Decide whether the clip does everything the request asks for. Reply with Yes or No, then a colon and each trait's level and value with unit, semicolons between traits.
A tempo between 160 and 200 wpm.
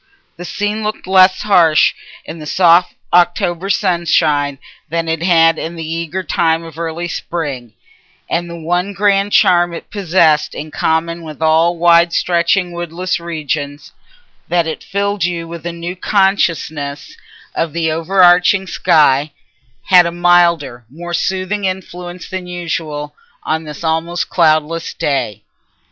No: slow, 135 wpm